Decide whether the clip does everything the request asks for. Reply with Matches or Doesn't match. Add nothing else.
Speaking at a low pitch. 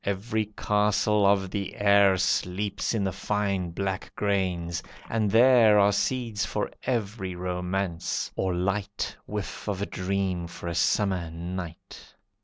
Matches